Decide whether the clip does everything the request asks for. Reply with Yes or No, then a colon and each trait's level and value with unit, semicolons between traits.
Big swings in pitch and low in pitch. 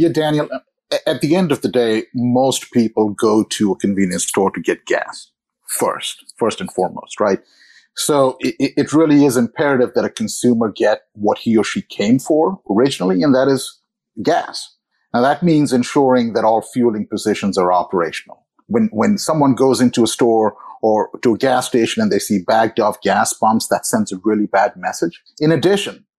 Yes: wide, 5.7 semitones; low, 125 Hz